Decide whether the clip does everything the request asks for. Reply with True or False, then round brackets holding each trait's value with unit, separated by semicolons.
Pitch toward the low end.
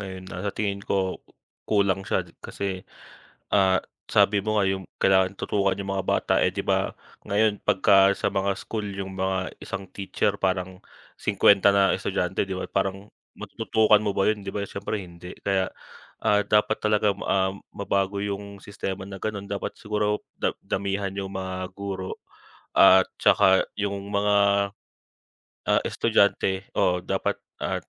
True (100 Hz)